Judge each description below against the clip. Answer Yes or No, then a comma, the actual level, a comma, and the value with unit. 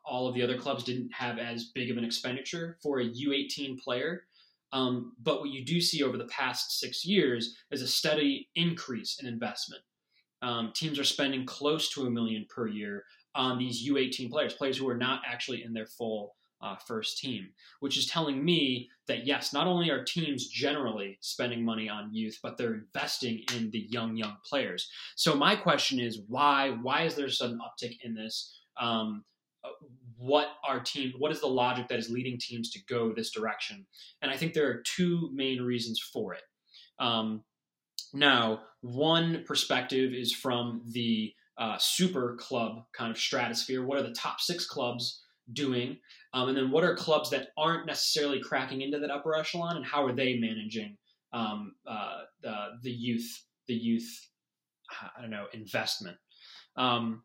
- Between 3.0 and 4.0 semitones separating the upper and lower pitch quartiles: Yes, average, 3.5 semitones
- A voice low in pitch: Yes, low, 125 Hz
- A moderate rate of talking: Yes, average, 180 wpm